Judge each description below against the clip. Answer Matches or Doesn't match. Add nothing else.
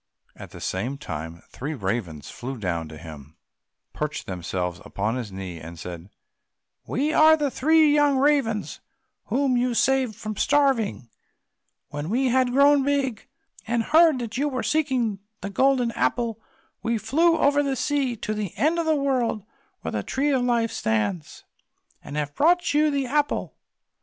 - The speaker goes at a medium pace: Matches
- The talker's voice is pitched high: Matches